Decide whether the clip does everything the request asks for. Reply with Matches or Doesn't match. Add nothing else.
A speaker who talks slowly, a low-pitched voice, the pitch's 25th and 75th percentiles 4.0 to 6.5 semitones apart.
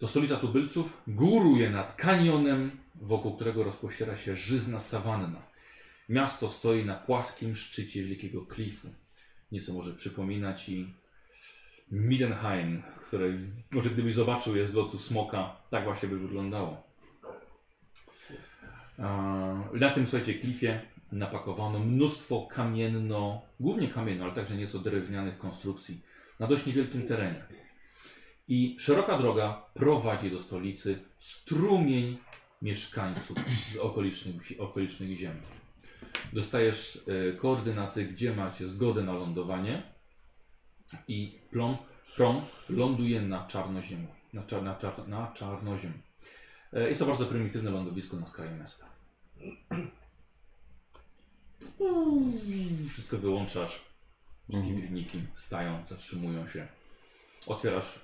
Matches